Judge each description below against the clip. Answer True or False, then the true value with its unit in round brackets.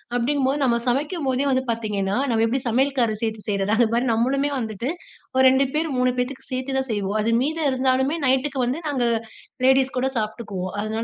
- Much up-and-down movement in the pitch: False (3.1 semitones)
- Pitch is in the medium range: False (255 Hz)